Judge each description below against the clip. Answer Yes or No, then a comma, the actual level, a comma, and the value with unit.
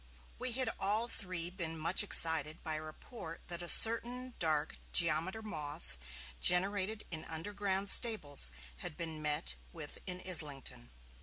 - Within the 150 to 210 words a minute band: No, average, 140 wpm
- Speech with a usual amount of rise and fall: Yes, average, 4.8 semitones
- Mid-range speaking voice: Yes, medium, 175 Hz